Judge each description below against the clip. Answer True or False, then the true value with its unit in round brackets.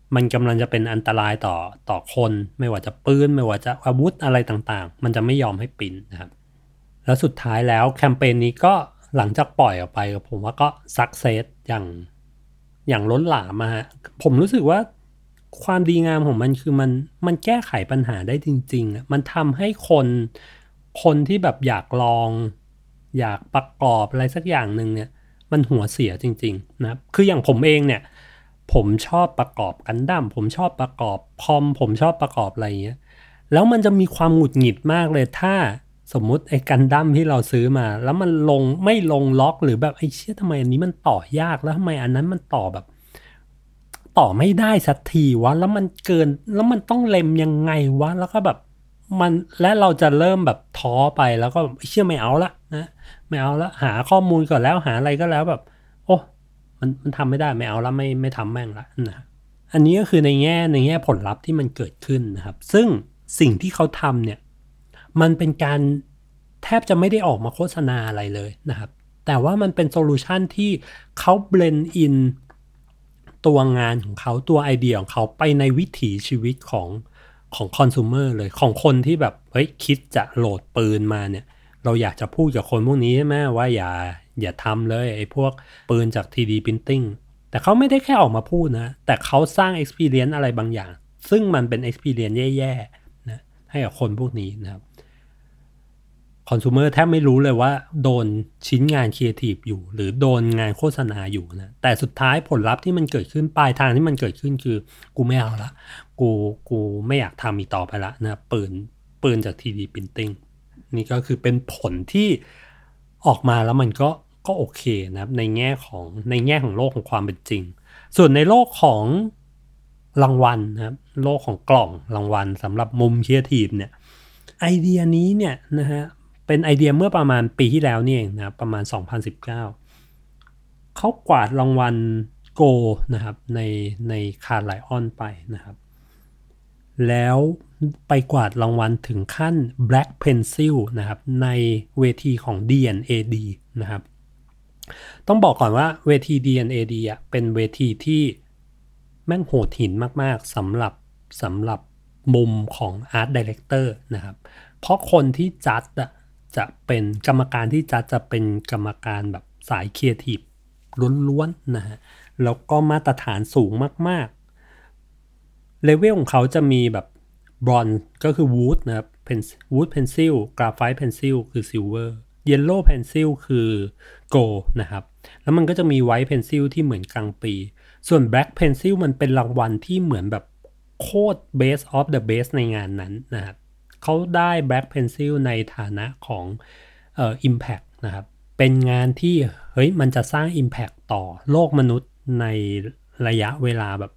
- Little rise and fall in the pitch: False (4.8 semitones)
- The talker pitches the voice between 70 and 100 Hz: False (130 Hz)